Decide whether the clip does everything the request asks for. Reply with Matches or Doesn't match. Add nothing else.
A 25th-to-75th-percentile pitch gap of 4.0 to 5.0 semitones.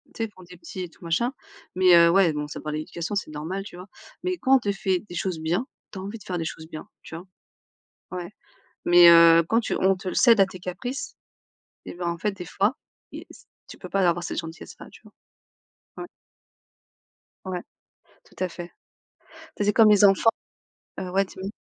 Doesn't match